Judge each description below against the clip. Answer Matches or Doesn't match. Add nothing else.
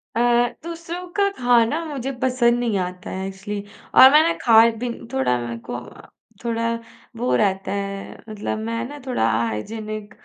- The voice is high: Matches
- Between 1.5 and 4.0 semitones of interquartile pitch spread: Doesn't match